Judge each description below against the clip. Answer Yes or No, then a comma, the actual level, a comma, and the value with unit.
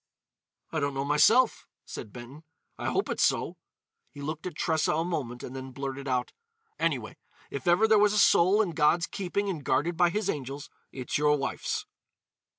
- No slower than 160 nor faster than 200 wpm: Yes, average, 180 wpm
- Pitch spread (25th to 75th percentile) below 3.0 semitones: No, average, 4.6 semitones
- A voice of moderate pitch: Yes, medium, 155 Hz